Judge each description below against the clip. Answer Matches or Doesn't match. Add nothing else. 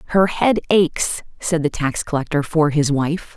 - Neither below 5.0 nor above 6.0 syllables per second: Doesn't match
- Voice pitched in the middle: Matches